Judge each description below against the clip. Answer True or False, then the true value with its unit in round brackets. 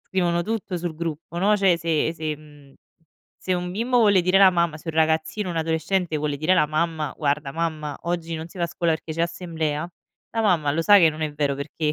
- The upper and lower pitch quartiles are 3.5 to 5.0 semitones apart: False (2.5 semitones)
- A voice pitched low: False (165 Hz)